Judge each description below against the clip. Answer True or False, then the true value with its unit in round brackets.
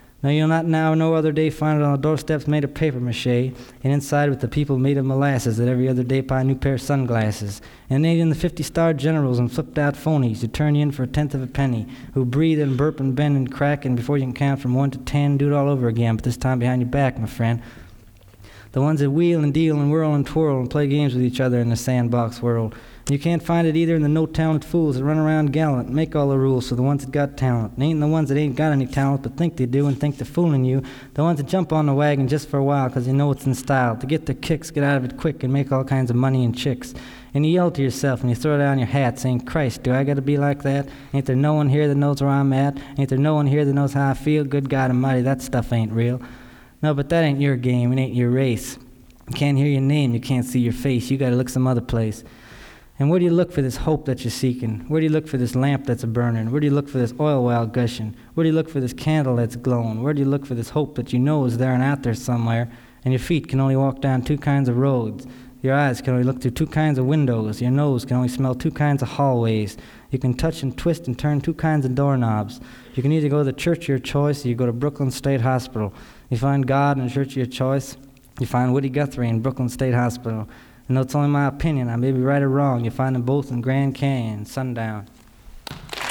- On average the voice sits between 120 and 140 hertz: True (135 Hz)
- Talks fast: True (280 wpm)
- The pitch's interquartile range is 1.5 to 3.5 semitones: True (2.6 semitones)